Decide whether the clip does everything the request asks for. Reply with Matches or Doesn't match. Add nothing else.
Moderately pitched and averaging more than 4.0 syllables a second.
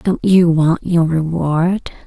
Doesn't match